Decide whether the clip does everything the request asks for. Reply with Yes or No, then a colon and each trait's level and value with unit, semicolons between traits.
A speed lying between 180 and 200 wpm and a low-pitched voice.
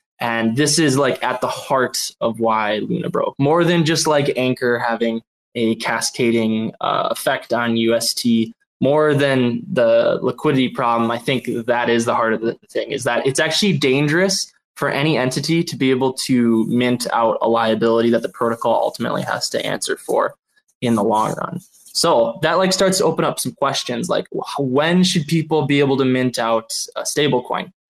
Yes: average, 185 wpm; low, 130 Hz